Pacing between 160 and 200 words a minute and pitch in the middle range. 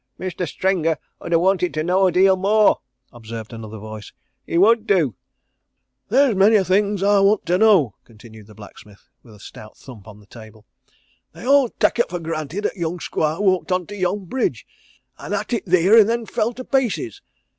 Yes: average, 195 wpm; medium, 180 Hz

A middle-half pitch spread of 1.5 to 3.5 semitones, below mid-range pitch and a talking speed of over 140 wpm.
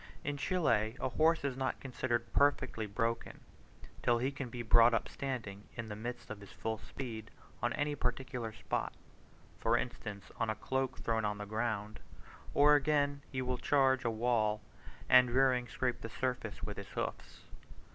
Yes: average, 3.1 semitones; low, 120 Hz; average, 170 wpm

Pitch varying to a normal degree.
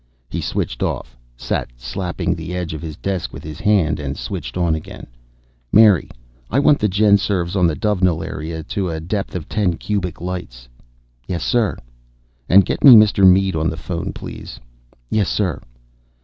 Yes: average, 3.8 semitones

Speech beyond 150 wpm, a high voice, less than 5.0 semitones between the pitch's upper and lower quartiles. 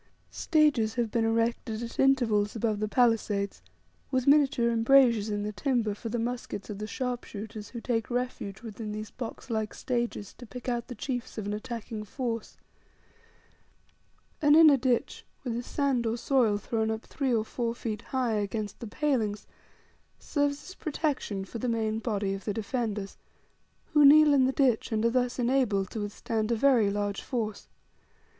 Yes: average, 170 wpm; high, 230 Hz; average, 3.1 semitones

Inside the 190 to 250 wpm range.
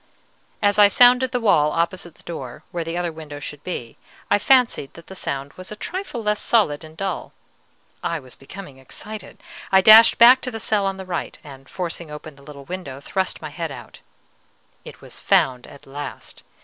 Yes: average, 195 wpm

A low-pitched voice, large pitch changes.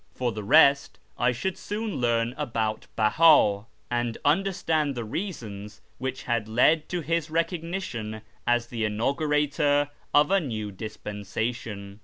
Yes: low, 125 Hz; wide, 6.1 semitones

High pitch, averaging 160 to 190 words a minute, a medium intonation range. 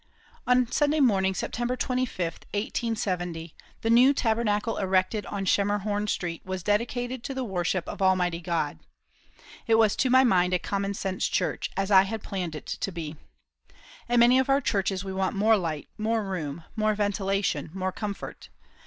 Yes: high, 200 Hz; average, 165 wpm; average, 3.6 semitones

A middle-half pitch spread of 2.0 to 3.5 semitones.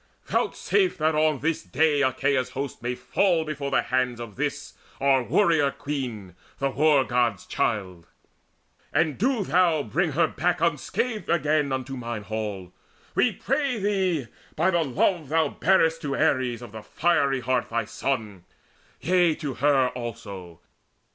No: average, 5.0 semitones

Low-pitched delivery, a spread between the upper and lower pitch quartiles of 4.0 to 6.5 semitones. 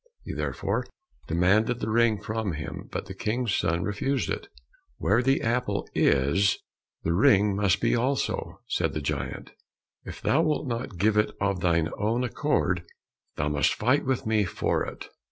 Yes: low, 105 Hz; average, 4.9 semitones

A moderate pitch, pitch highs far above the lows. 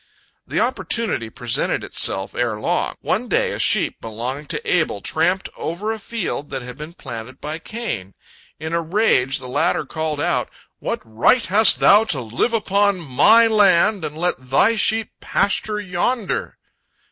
Yes: medium, 165 Hz; wide, 8.4 semitones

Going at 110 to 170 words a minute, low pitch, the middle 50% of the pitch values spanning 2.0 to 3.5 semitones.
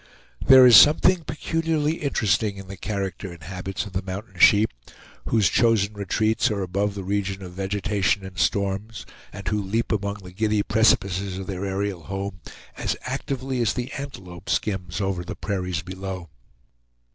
Yes: average, 160 wpm; low, 100 Hz; narrow, 2.6 semitones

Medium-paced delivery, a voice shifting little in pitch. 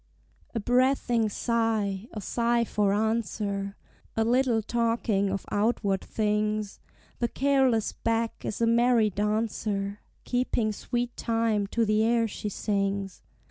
No: slow, 125 wpm; narrow, 2.2 semitones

